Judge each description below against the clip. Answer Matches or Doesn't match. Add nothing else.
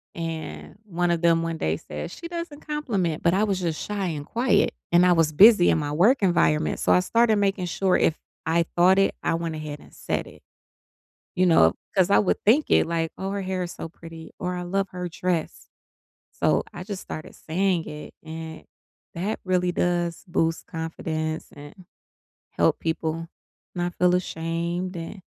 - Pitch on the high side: Doesn't match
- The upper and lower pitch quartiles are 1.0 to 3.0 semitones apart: Matches